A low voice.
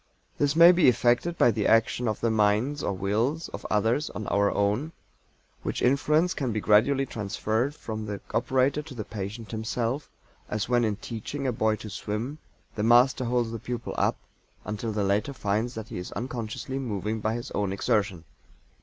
Yes: low, 115 Hz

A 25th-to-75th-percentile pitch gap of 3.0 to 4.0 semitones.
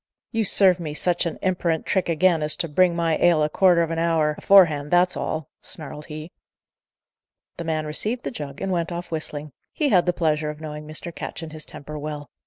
No: narrow, 2.6 semitones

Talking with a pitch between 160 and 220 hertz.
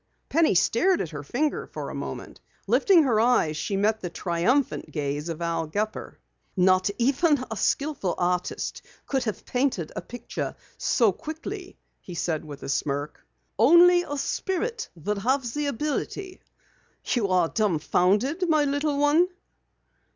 No: high, 235 Hz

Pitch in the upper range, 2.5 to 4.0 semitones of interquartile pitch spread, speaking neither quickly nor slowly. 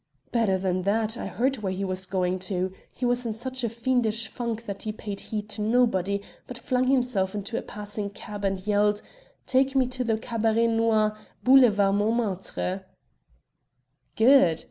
Yes: high, 215 Hz; average, 3.3 semitones; average, 165 wpm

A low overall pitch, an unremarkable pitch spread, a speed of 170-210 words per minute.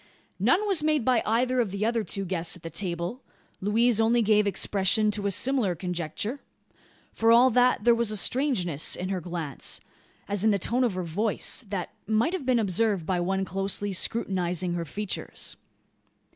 No: high, 205 Hz; average, 4.3 semitones; average, 180 wpm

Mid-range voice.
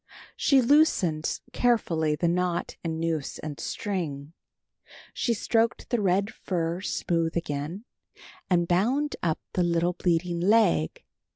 Yes: medium, 175 Hz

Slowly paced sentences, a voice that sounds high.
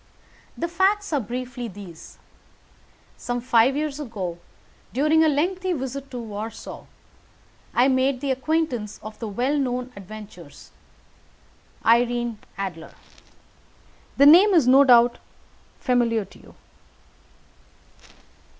Yes: slow, 110 wpm; very high, 250 Hz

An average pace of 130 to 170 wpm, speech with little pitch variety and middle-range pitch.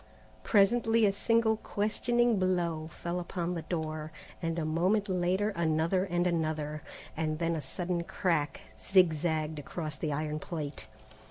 No: average, 140 wpm; average, 3.4 semitones; medium, 170 Hz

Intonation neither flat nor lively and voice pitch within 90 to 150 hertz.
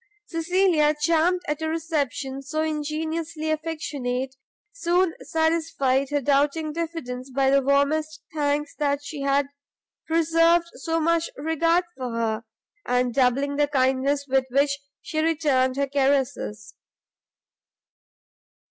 No: average, 3.0 semitones; very high, 295 Hz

